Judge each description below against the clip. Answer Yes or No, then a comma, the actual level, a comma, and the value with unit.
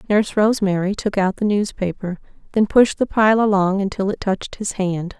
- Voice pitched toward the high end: Yes, high, 200 Hz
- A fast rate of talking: No, average, 185 wpm